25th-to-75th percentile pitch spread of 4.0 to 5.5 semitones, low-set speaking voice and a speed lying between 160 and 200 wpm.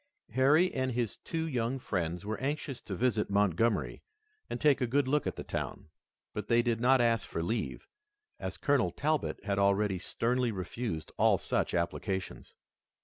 Yes: average, 4.8 semitones; low, 115 Hz; average, 165 wpm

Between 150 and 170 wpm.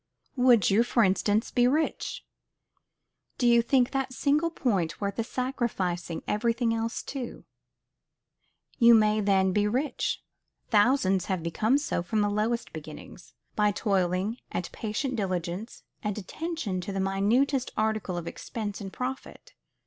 No: average, 140 wpm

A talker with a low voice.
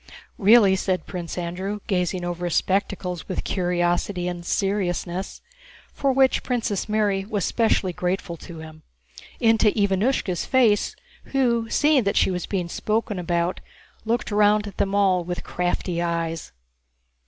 No: high, 190 Hz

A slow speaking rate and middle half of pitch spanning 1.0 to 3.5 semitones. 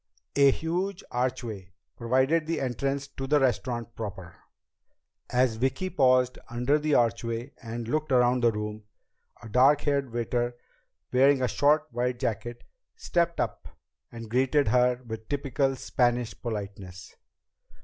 Yes: slow, 130 wpm; average, 3.2 semitones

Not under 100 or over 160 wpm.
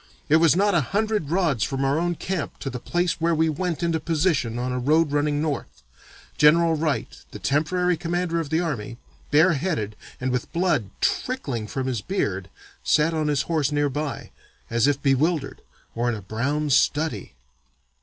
No: average, 175 wpm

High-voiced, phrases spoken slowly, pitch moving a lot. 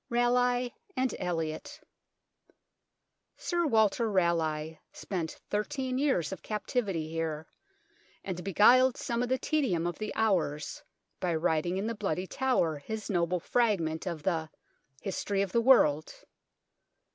Yes: high, 195 Hz; slow, 130 wpm; wide, 6.7 semitones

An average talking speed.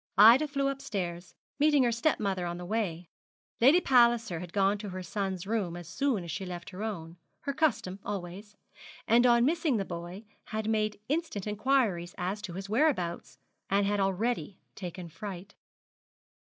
Yes: average, 170 wpm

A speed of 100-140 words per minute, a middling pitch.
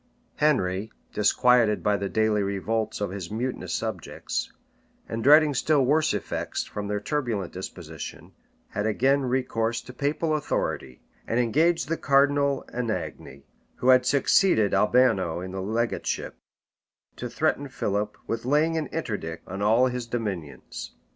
No: slow, 135 wpm; low, 115 Hz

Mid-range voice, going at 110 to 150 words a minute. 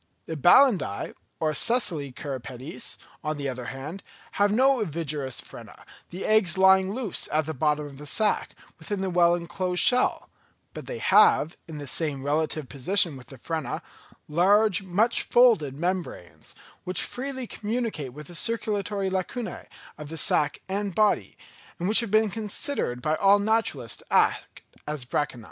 No: medium, 175 Hz; average, 160 wpm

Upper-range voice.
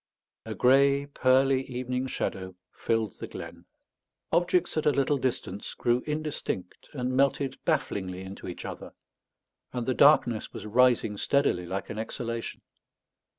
No: low, 125 Hz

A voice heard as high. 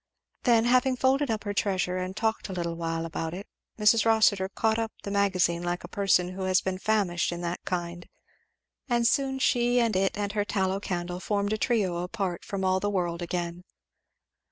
Yes: high, 195 Hz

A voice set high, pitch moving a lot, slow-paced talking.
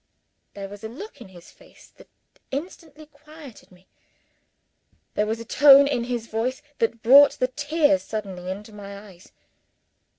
No: high, 235 Hz; wide, 5.8 semitones; average, 155 wpm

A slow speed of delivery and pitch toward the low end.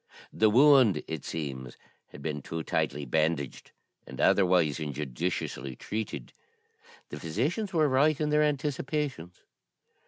Yes: slow, 120 wpm; very low, 90 Hz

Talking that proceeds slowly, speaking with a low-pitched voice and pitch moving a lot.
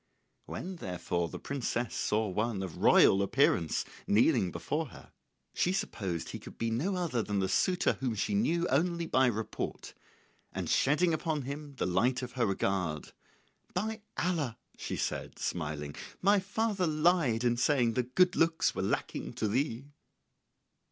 No: average, 155 wpm; low, 125 Hz; wide, 8.1 semitones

